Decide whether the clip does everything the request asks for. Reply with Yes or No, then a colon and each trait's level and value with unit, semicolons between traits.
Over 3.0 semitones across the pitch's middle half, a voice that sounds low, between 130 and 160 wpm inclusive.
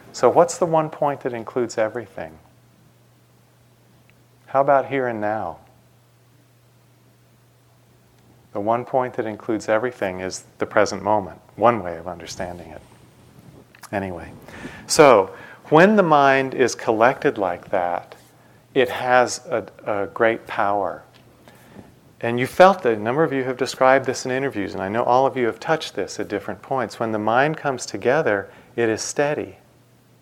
Yes: average, 4.5 semitones; low, 120 Hz; average, 150 wpm